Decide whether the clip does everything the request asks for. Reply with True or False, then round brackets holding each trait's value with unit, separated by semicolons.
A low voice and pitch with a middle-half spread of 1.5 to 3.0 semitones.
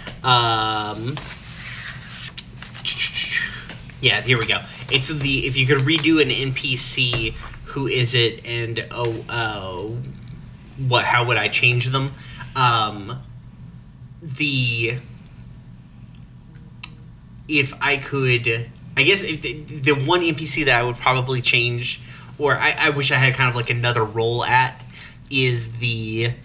True (125 Hz; 2.5 semitones)